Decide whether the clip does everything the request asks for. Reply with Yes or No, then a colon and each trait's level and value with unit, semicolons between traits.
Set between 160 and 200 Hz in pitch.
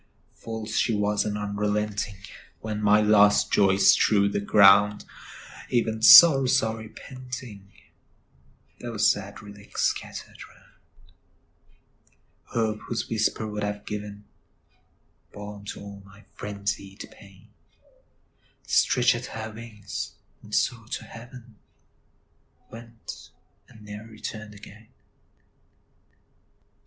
No: low, 105 Hz